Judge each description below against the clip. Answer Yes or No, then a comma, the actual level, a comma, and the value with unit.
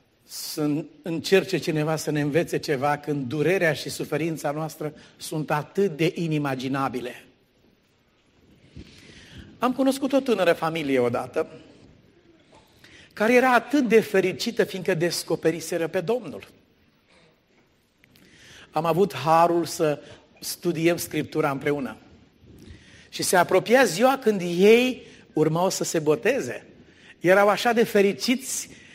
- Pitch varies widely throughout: No, average, 4.7 semitones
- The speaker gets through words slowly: Yes, slow, 110 wpm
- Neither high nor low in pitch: Yes, medium, 165 Hz